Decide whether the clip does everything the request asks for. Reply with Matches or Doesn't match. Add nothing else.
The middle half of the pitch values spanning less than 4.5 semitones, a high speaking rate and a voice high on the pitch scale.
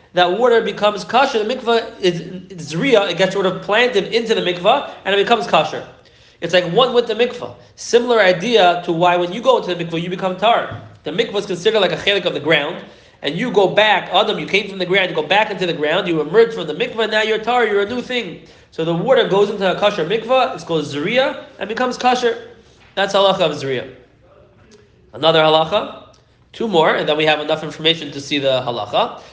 Doesn't match